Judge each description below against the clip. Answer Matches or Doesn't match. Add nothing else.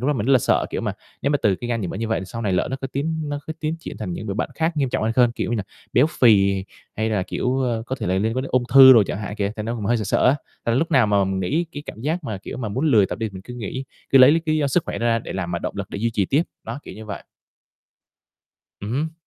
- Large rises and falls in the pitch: Doesn't match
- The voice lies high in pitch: Doesn't match